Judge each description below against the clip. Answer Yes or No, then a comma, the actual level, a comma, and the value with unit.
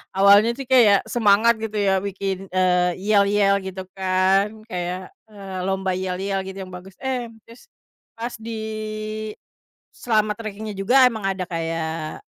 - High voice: Yes, high, 195 Hz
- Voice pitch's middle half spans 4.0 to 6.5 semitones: No, narrow, 2.6 semitones